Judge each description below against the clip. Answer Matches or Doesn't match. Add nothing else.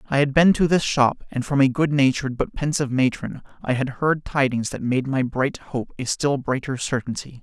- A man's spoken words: Matches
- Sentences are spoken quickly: Matches